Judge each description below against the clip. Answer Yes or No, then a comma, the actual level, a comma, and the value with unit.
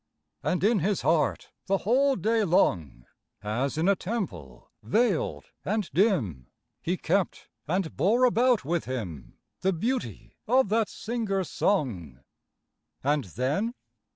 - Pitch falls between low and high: Yes, medium, 180 Hz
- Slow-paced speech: Yes, slow, 125 wpm